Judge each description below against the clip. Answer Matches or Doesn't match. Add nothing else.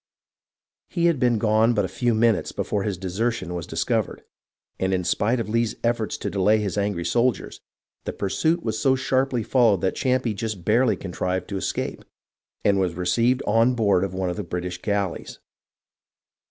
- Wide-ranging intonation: Doesn't match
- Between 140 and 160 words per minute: Doesn't match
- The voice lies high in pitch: Doesn't match